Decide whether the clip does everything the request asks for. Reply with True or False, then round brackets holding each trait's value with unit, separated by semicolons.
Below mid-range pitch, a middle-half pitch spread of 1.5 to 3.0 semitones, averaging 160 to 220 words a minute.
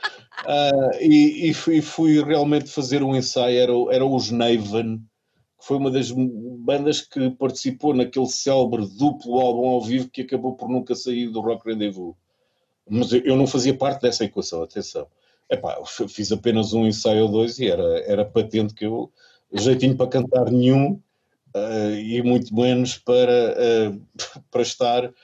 True (125 Hz; 2.6 semitones; 170 wpm)